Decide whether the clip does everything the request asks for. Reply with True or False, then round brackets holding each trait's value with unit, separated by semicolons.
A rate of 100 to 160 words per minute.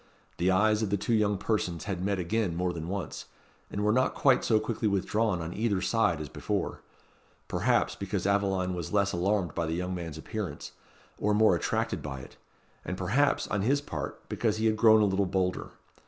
False (200 wpm)